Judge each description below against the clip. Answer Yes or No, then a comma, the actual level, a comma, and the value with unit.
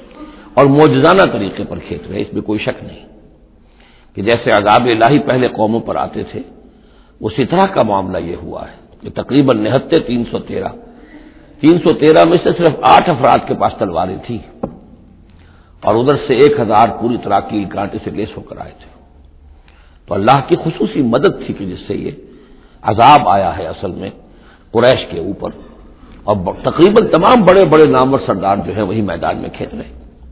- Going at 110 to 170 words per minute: No, average, 185 wpm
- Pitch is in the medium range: No, low, 110 Hz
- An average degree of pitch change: No, wide, 7.8 semitones